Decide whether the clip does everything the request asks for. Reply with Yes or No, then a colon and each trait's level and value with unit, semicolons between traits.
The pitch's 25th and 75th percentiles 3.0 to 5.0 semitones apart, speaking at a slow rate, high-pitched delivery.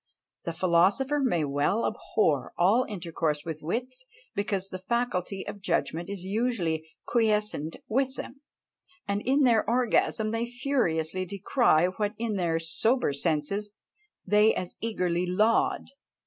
No: wide, 5.4 semitones; slow, 130 wpm; high, 200 Hz